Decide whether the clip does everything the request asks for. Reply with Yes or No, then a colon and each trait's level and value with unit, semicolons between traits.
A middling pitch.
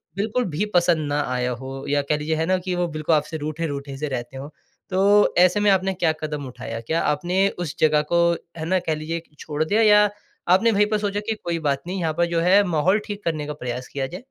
Yes: medium, 165 Hz